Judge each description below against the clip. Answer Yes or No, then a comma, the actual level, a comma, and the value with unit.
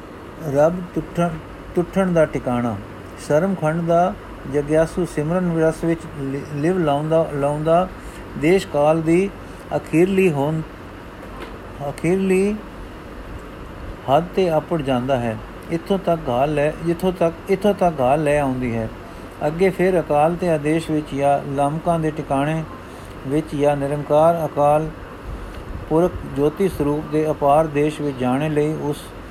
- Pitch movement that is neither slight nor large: Yes, average, 3.2 semitones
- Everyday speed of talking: Yes, average, 125 wpm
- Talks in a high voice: No, medium, 150 Hz